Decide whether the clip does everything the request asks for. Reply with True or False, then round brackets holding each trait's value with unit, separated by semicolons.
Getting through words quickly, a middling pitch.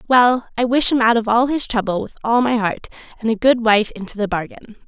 False (245 wpm; 230 Hz)